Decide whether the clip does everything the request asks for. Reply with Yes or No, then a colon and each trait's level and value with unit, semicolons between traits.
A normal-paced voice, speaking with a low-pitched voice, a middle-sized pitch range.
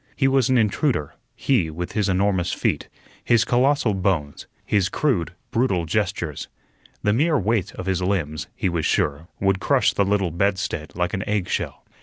Yes: average, 170 wpm; very low, 95 Hz; average, 4.5 semitones